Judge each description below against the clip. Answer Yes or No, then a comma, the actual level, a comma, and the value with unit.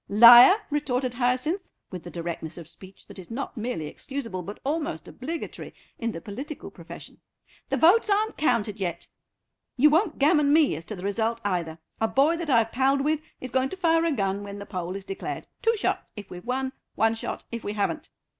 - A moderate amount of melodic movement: No, wide, 6.9 semitones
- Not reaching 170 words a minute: No, average, 200 wpm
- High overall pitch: Yes, high, 240 Hz